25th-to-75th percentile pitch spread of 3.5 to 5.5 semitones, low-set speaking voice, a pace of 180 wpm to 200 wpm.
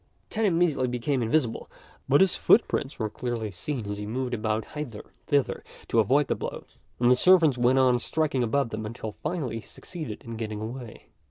Yes: average, 4.7 semitones; low, 125 Hz; average, 190 wpm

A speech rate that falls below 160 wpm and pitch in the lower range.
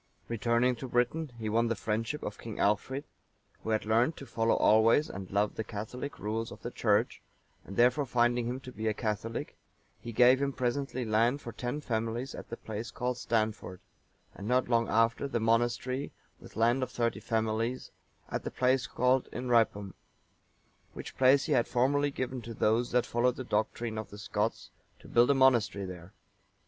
No: average, 180 wpm; low, 120 Hz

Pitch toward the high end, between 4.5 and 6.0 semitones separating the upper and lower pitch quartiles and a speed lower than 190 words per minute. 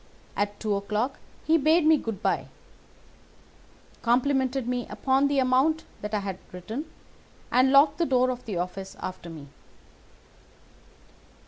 Yes: very high, 250 Hz; average, 5.3 semitones; slow, 135 wpm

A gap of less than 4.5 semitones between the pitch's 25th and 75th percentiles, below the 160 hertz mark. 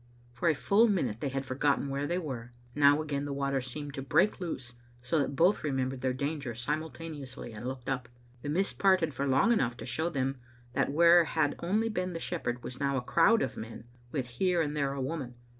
Yes: average, 4.1 semitones; medium, 140 Hz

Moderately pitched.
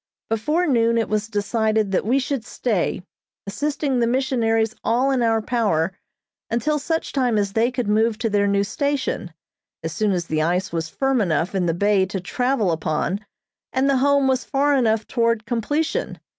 No: high, 225 Hz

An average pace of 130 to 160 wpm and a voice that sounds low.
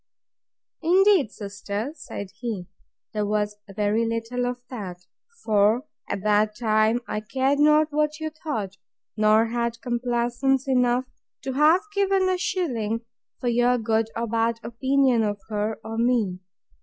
No: average, 140 wpm; high, 235 Hz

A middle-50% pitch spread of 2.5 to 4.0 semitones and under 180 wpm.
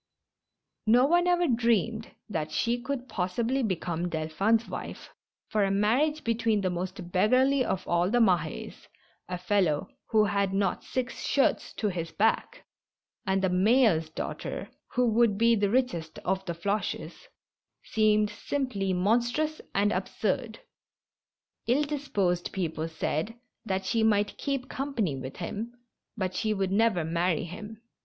No: average, 4.7 semitones; average, 145 wpm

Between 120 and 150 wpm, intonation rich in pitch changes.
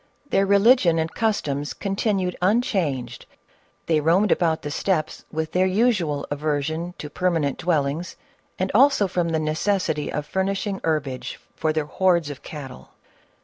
No: average, 145 wpm; average, 4.3 semitones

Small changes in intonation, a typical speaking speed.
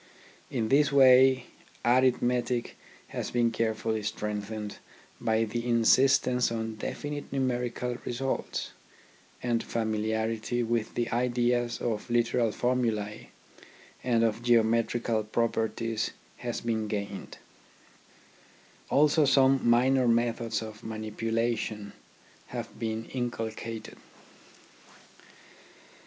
No: narrow, 1.9 semitones; slow, 90 wpm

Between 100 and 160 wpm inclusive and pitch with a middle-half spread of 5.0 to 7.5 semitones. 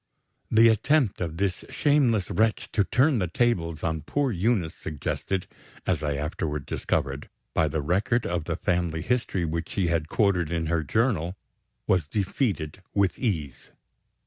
Yes: average, 145 wpm; wide, 5.6 semitones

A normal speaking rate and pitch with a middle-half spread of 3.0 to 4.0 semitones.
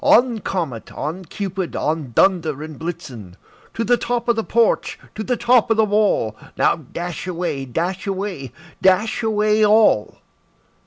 No: average, 155 wpm; wide, 5.6 semitones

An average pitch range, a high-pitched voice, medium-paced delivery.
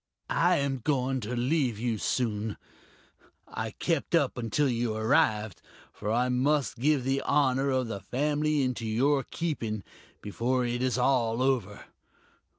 No: average, 3.6 semitones; low, 125 Hz; average, 145 wpm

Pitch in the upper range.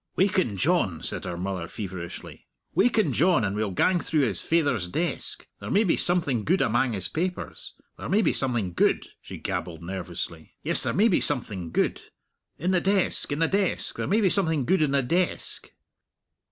No: medium, 140 Hz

